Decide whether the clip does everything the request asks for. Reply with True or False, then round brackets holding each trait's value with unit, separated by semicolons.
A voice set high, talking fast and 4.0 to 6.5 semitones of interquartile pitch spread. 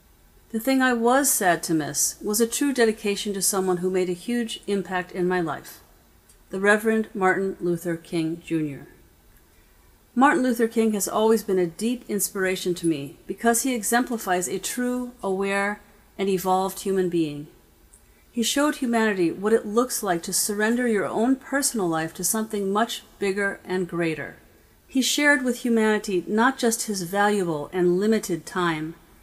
False (200 Hz; 160 wpm; 4.3 semitones)